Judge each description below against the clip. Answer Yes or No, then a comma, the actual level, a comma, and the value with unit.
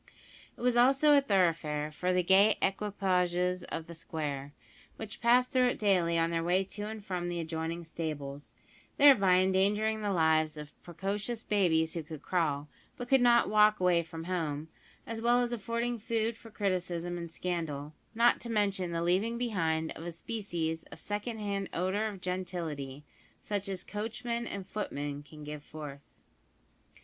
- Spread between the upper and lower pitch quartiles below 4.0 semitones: No, average, 4.8 semitones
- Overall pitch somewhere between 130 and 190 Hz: Yes, medium, 185 Hz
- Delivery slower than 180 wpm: Yes, average, 165 wpm